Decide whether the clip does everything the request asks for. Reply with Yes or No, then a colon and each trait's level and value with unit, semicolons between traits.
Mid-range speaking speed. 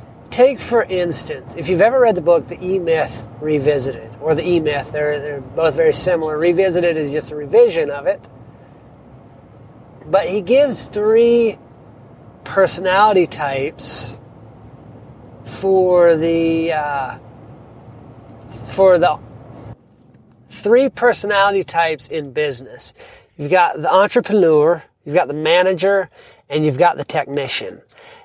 No: slow, 125 wpm